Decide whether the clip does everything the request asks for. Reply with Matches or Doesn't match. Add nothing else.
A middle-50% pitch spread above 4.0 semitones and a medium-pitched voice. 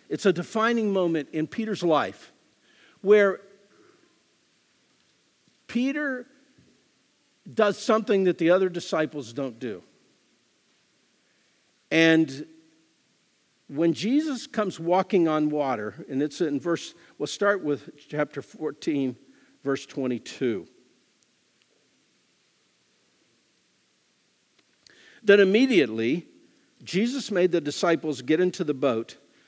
Matches